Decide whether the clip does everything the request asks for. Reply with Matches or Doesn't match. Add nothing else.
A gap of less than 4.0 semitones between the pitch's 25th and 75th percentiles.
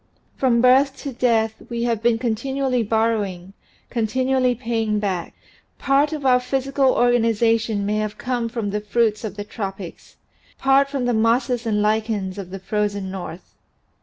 Matches